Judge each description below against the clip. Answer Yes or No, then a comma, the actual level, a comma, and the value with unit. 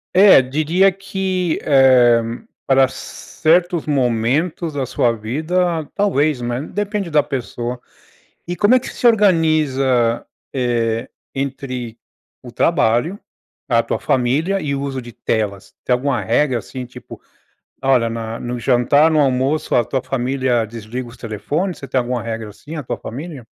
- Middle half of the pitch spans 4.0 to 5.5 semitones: Yes, average, 4.7 semitones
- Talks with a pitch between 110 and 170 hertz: Yes, low, 135 Hz